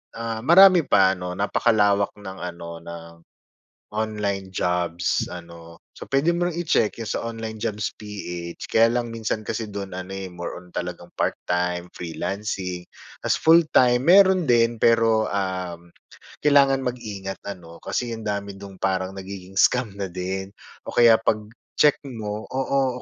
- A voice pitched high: No, low, 105 Hz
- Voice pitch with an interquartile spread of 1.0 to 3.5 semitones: No, average, 4.2 semitones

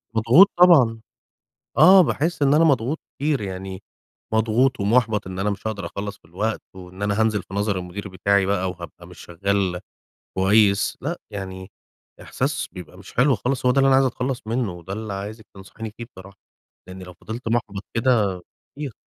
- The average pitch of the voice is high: No, low, 105 Hz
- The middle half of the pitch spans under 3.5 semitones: No, average, 4.7 semitones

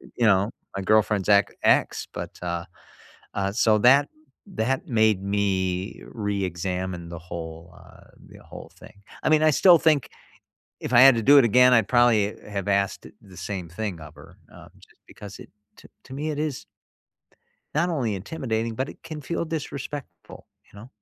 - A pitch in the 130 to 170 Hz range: No, low, 105 Hz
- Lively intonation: Yes, wide, 5.9 semitones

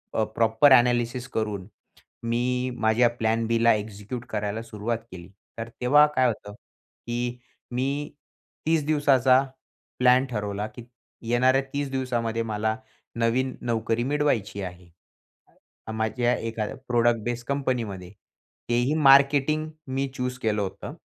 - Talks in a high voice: No, low, 120 Hz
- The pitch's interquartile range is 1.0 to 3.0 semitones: Yes, average, 2.7 semitones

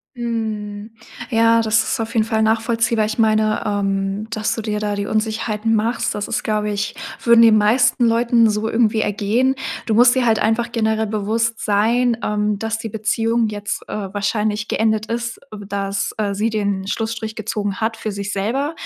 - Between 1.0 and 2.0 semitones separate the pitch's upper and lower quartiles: Yes, narrow, 1.5 semitones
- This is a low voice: No, high, 220 Hz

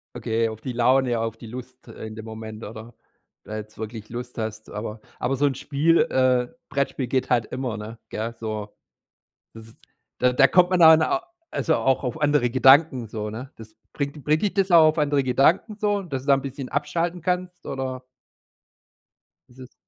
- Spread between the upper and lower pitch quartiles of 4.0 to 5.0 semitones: Yes, average, 4.6 semitones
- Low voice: Yes, low, 130 Hz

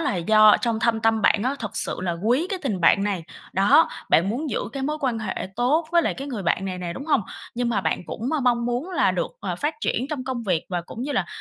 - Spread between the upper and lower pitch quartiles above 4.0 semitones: Yes, wide, 5.5 semitones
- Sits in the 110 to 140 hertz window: No, high, 235 Hz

